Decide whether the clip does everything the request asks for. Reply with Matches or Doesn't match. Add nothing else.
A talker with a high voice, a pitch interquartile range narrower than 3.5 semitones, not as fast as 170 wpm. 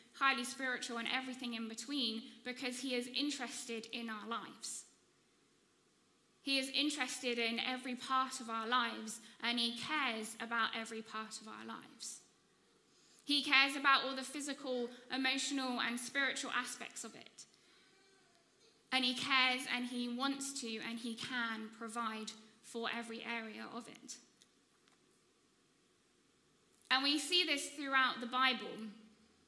Matches